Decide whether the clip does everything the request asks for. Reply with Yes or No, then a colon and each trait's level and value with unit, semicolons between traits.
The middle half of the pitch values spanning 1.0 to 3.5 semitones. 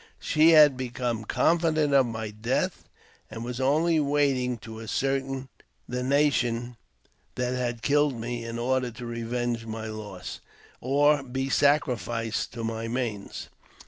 Yes: average, 3.1 semitones